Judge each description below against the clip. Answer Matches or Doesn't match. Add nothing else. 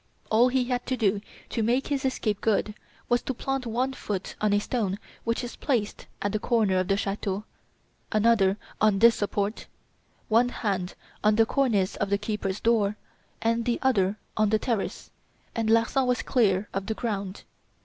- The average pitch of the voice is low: Doesn't match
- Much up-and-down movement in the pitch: Doesn't match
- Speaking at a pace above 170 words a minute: Matches